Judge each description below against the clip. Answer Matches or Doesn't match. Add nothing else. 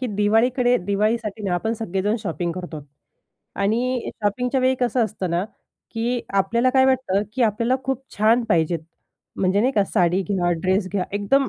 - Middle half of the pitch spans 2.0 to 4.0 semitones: Doesn't match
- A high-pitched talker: Matches